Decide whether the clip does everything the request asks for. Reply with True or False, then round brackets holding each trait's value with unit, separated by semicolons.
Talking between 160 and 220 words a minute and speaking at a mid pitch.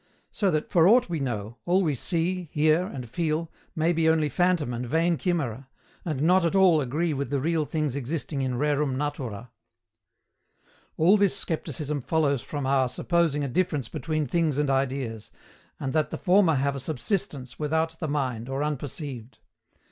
True (170 wpm; 150 Hz)